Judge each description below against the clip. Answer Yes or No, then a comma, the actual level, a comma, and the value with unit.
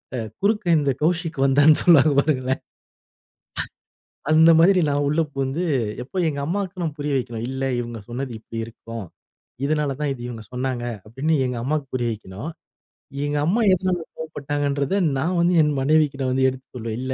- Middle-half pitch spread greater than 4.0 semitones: No, average, 3.7 semitones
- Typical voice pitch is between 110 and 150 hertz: Yes, medium, 140 Hz